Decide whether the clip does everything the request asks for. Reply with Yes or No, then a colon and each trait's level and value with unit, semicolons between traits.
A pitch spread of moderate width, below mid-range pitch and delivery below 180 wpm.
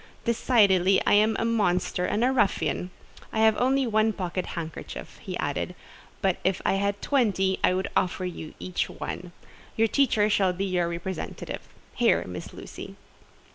No: average, 3.4 semitones; high, 195 Hz; average, 160 wpm